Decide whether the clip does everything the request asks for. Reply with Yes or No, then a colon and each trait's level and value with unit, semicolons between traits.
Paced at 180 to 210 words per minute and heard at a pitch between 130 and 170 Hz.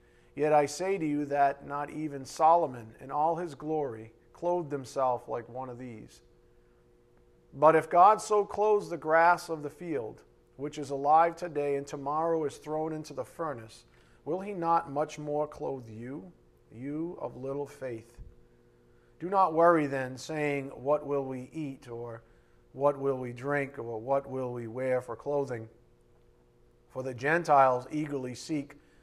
No: average, 160 wpm; medium, 140 Hz